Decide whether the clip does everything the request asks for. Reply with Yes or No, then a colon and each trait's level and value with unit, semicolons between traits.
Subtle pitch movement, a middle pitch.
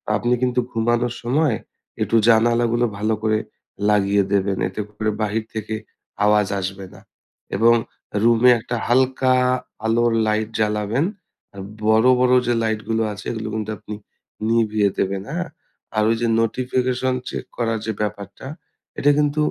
No: narrow, 2.3 semitones; low, 110 Hz